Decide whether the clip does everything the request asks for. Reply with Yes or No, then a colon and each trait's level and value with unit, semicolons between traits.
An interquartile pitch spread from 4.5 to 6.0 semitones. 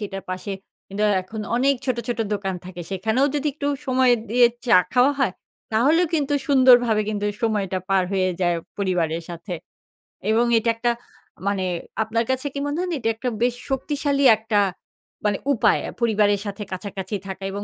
Yes: average, 4.8 semitones